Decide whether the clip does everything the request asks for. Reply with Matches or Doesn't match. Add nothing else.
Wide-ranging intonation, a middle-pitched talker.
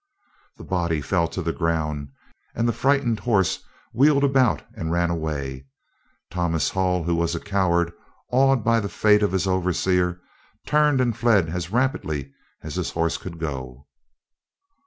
Doesn't match